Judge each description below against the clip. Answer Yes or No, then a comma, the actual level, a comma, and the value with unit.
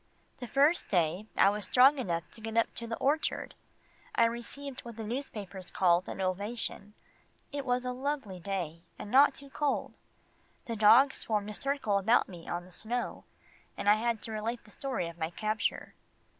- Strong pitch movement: No, average, 4.4 semitones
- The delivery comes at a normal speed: Yes, average, 185 wpm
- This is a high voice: Yes, high, 220 Hz